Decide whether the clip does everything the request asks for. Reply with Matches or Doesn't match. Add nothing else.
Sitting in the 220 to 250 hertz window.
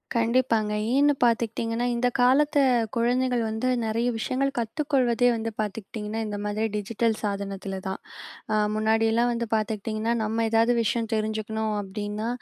Matches